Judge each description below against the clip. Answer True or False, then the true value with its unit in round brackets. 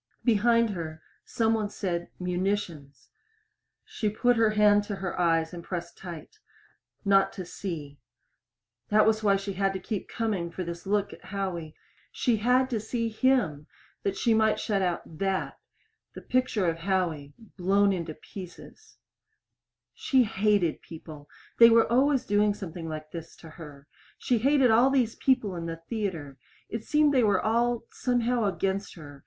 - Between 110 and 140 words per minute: False (160 wpm)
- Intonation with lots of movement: False (4.8 semitones)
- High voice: True (200 Hz)